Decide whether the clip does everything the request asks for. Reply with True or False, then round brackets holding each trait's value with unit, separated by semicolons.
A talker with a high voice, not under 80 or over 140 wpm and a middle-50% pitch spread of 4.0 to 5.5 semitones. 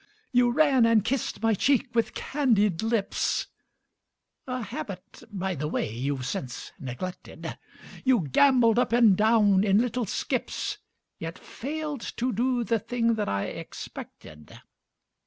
True (225 Hz; 135 wpm; 4.7 semitones)